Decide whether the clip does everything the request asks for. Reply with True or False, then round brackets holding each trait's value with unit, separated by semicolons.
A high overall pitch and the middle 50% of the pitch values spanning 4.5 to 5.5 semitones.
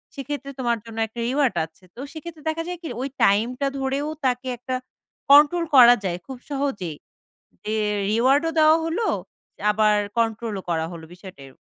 True (250 Hz; 5.2 semitones)